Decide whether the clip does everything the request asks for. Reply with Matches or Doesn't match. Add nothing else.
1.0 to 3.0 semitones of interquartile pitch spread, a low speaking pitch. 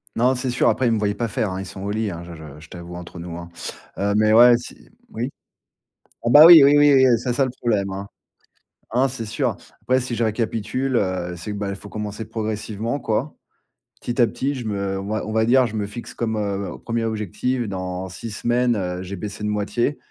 Doesn't match